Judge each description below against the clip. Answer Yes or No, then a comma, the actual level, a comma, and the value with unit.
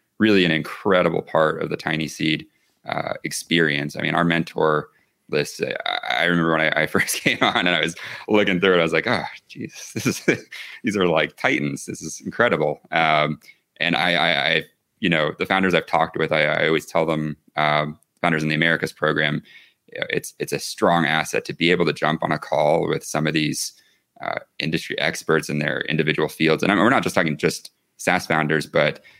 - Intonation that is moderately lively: No, narrow, 1.8 semitones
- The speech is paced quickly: Yes, fast, 210 wpm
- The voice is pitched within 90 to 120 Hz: No, very low, 80 Hz